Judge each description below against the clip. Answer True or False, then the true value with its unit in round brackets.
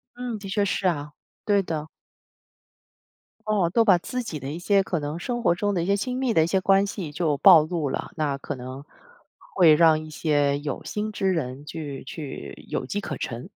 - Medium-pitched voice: True (170 Hz)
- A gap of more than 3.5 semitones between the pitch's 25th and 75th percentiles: True (5.1 semitones)